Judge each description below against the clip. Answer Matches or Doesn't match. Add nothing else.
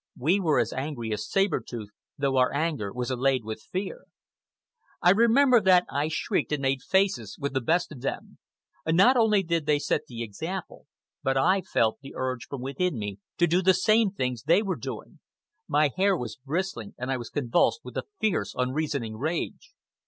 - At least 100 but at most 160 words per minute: Doesn't match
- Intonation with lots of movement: Matches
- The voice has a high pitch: Doesn't match